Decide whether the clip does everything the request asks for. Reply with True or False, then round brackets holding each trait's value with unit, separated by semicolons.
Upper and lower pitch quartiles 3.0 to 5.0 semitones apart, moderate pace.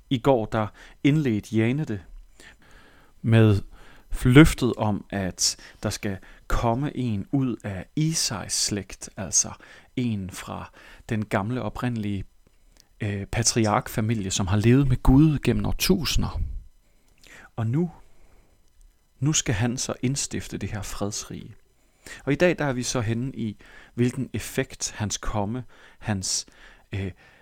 False (4.3 semitones; 125 wpm)